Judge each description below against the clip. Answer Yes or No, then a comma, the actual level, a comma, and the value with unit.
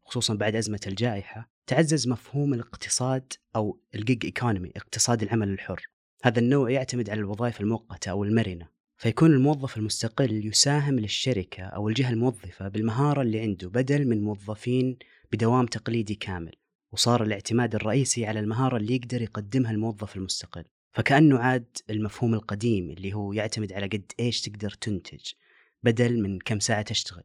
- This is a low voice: Yes, low, 115 Hz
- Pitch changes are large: No, average, 3.1 semitones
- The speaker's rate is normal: No, fast, 145 wpm